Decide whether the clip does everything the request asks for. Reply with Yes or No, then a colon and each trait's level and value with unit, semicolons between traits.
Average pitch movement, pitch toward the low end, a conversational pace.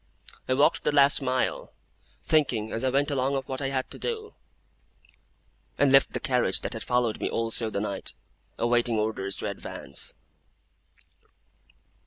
Yes: average, 3.4 semitones; low, 130 Hz; average, 160 wpm